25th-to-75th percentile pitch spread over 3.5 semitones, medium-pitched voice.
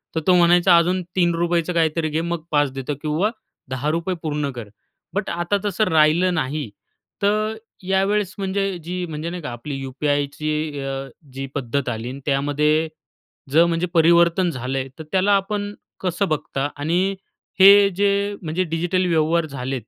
Yes: average, 4.1 semitones; medium, 165 Hz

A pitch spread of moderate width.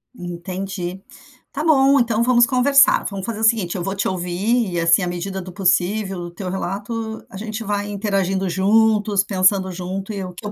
Yes: average, 3.1 semitones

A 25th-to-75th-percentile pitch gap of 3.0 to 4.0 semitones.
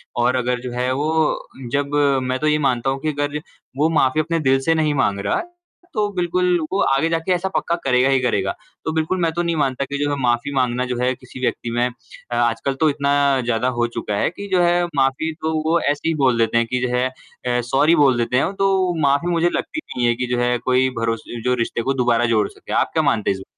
No: average, 4.5 semitones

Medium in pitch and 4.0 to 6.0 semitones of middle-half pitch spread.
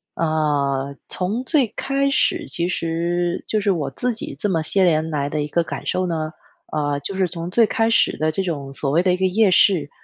Yes: medium, 170 Hz; average, 4.3 semitones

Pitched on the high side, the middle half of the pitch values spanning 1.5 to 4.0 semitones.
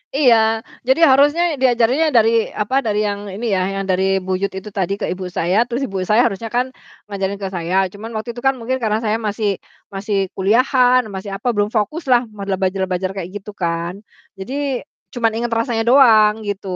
Yes: high, 210 Hz; average, 3.7 semitones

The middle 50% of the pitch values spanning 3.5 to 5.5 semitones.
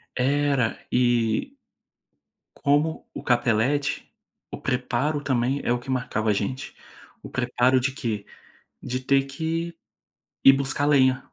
No: average, 2.7 semitones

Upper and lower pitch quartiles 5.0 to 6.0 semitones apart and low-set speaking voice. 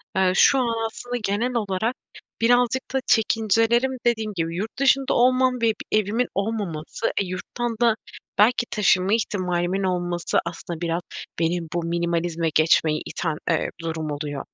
No: wide, 5.4 semitones; high, 195 Hz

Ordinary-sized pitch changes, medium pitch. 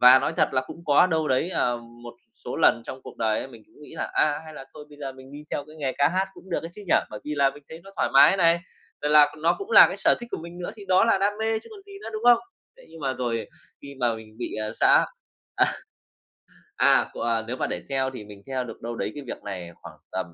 No: wide, 5.7 semitones; medium, 145 Hz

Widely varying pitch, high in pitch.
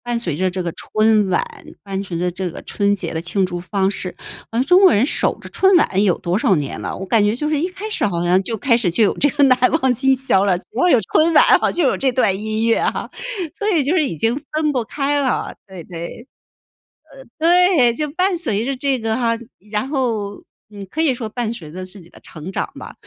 Yes: wide, 6.7 semitones; high, 230 Hz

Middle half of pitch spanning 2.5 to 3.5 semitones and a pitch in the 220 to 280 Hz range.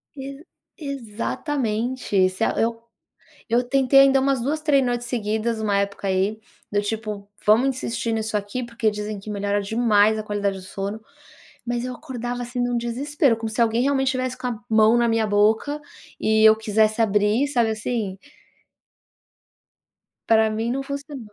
Yes: average, 3.1 semitones; high, 225 Hz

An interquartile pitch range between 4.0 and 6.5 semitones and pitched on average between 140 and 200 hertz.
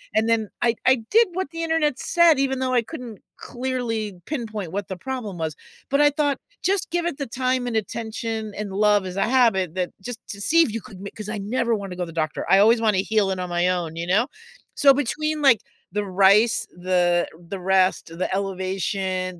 No: average, 5.3 semitones; high, 215 Hz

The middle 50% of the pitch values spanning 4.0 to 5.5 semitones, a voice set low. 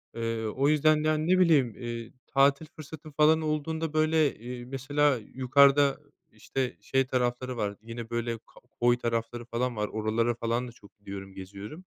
Yes: average, 4.3 semitones; low, 125 Hz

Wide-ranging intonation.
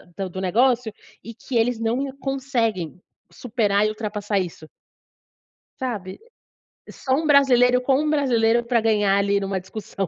No: average, 4.1 semitones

